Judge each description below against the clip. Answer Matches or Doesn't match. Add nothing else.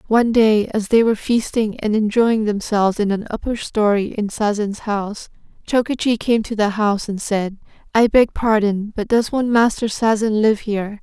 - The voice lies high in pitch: Matches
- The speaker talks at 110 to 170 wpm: Doesn't match